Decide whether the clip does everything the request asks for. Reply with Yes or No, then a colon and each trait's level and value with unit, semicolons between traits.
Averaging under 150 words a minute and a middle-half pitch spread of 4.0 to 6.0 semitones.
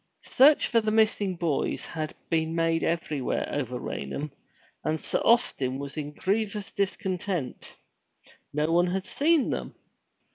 Yes: slow, 135 wpm; average, 5.3 semitones